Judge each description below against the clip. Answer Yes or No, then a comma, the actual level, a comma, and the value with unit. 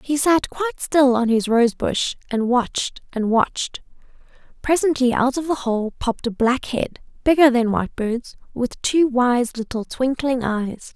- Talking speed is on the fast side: No, average, 165 wpm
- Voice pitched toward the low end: No, very high, 255 Hz